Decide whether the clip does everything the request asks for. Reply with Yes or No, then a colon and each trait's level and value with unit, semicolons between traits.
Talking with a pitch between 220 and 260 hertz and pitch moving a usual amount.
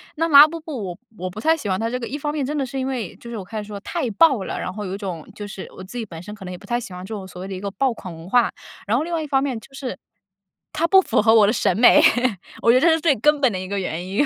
No: high, 225 Hz; wide, 6.3 semitones